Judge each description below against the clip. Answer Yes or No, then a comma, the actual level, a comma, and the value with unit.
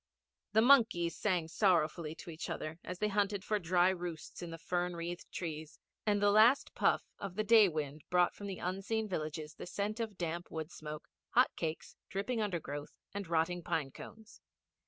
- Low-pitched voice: No, medium, 180 Hz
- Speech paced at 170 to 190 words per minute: Yes, average, 180 wpm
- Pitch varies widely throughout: No, average, 4.0 semitones